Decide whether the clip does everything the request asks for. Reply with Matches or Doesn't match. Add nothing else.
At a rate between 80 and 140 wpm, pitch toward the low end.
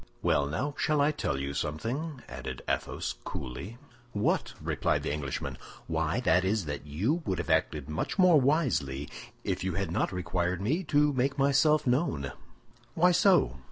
Doesn't match